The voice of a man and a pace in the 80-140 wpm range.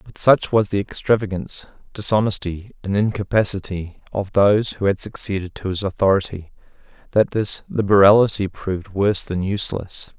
Yes: male; slow, 135 wpm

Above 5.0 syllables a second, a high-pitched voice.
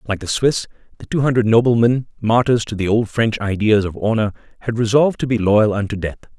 No: 5.9 syllables/s; low, 110 Hz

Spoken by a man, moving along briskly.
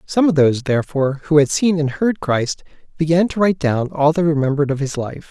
Yes: male; fast, 225 wpm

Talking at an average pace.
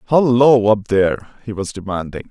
Yes: average, 155 wpm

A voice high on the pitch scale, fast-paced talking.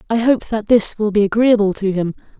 Yes: high, 210 Hz; fast, 225 wpm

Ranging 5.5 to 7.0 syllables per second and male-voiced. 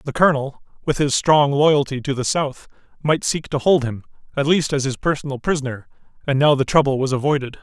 Yes: 5.8 syllables/s; male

